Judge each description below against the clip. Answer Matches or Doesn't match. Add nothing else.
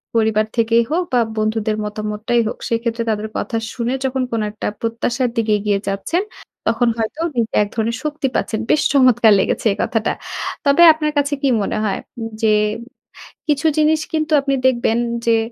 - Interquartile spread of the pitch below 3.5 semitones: Doesn't match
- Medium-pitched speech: Doesn't match